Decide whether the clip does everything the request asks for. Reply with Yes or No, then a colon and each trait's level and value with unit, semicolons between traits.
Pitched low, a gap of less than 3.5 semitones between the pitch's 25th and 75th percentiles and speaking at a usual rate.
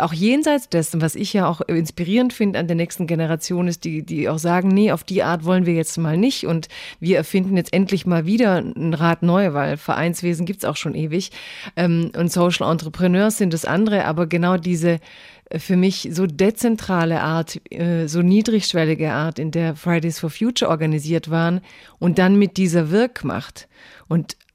No: medium, 175 Hz; narrow, 2.5 semitones; average, 180 wpm